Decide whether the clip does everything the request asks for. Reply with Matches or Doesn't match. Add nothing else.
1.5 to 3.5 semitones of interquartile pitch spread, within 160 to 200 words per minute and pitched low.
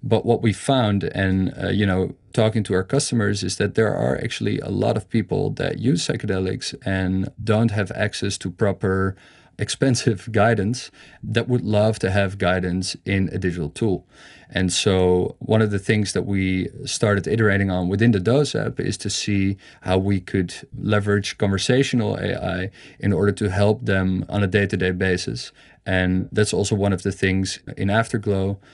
Matches